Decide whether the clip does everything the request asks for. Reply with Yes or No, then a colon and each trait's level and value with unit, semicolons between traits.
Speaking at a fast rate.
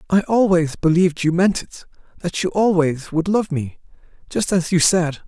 No: average, 180 wpm